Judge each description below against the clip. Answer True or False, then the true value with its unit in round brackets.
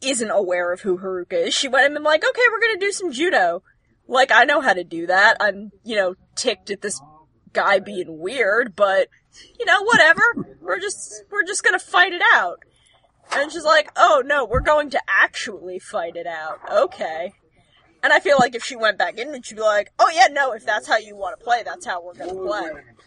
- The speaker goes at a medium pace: False (220 wpm)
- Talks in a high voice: True (230 Hz)